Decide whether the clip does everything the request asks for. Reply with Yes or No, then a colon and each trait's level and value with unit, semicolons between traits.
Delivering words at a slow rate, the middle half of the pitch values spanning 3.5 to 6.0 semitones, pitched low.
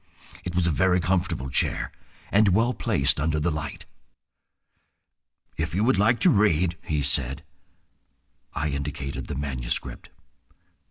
Yes: slow, 130 wpm; average, 5.1 semitones; very low, 80 Hz